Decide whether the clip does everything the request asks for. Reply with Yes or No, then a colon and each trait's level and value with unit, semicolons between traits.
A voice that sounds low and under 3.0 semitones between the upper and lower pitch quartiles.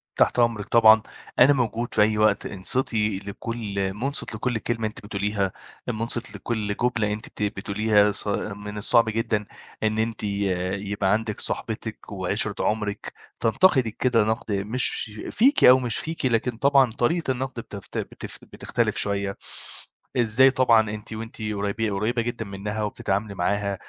Yes: low, 110 Hz; narrow, 2.5 semitones